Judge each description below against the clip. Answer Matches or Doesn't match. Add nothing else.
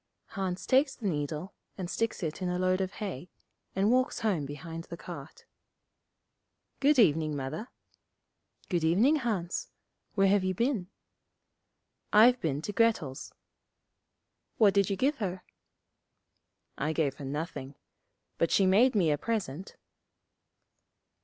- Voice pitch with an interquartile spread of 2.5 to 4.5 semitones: Doesn't match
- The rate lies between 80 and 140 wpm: Matches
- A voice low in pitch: Doesn't match